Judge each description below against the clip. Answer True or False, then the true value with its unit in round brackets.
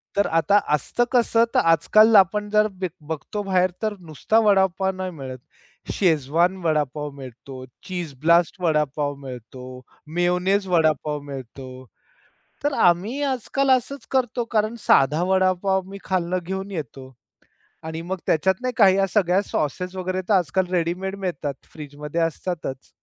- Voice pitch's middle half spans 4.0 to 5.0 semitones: True (4.4 semitones)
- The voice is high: False (180 Hz)